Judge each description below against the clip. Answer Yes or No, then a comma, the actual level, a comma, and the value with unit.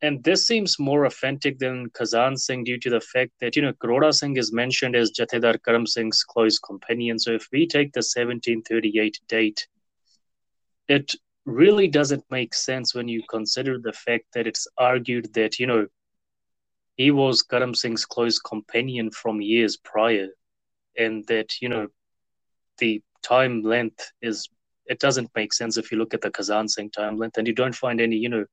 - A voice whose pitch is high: No, low, 115 Hz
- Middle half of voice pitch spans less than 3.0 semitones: Yes, narrow, 2.5 semitones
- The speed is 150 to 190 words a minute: Yes, average, 180 wpm